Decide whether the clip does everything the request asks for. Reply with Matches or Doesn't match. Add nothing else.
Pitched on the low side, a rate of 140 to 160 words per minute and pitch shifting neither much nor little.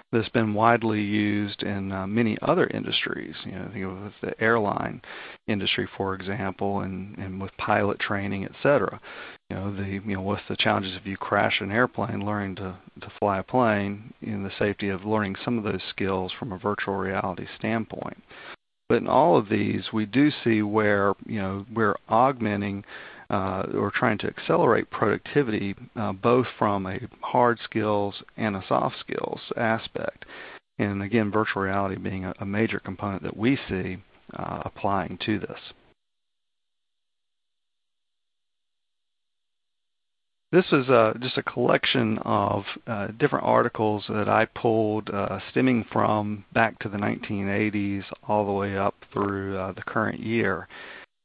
Doesn't match